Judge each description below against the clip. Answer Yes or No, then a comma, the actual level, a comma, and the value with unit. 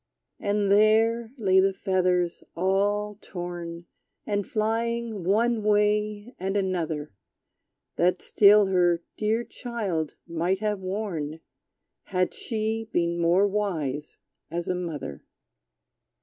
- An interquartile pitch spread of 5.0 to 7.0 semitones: No, average, 3.3 semitones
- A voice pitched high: Yes, high, 195 Hz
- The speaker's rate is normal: No, slow, 105 wpm